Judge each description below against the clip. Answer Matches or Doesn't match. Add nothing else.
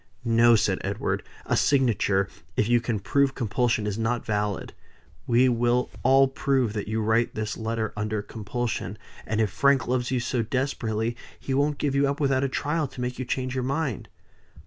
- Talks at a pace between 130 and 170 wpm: Doesn't match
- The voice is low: Matches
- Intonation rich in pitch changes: Doesn't match